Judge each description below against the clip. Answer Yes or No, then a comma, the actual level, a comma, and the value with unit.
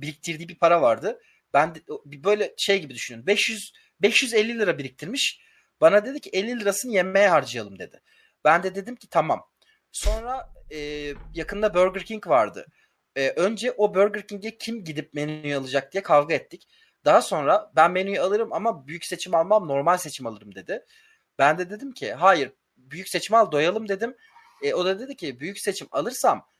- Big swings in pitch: Yes, wide, 6.3 semitones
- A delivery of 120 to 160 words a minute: No, average, 170 wpm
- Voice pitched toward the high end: Yes, high, 200 Hz